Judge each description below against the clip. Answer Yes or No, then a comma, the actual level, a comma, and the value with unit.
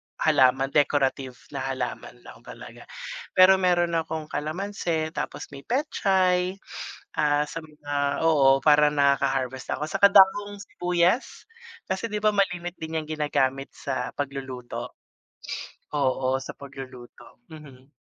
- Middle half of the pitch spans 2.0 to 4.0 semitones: No, average, 4.8 semitones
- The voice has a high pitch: No, medium, 150 Hz